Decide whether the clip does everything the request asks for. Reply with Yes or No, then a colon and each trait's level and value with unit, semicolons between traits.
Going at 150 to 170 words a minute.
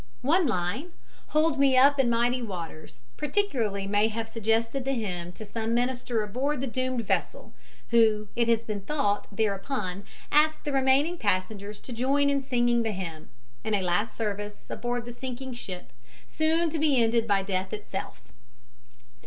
Yes: average, 160 wpm